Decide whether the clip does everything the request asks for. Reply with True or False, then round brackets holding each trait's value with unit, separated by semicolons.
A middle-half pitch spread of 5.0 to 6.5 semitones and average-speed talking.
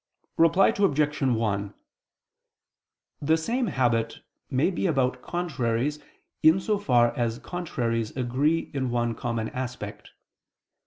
False (5.5 semitones; 110 wpm)